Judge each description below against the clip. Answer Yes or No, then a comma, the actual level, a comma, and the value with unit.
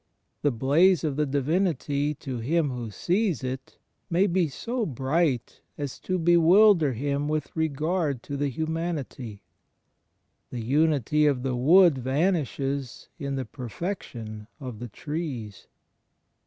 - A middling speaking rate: No, slow, 130 wpm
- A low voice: No, medium, 145 Hz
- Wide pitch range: No, average, 4.4 semitones